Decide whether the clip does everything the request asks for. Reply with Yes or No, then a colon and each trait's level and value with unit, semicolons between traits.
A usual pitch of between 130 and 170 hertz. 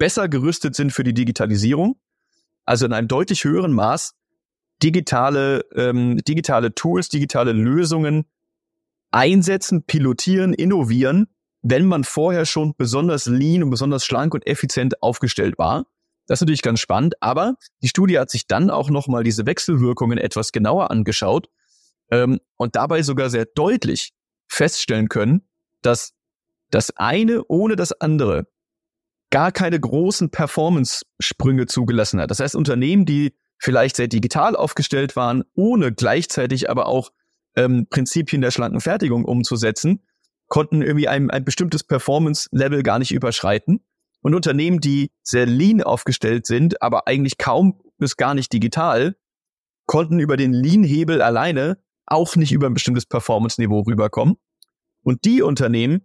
Yes: medium, 140 Hz